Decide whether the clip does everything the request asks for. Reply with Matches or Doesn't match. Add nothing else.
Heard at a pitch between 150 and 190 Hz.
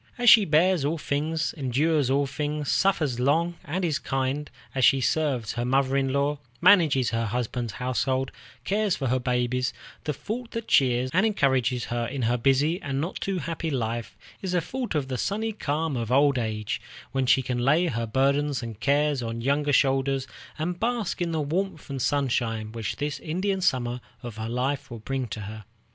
Doesn't match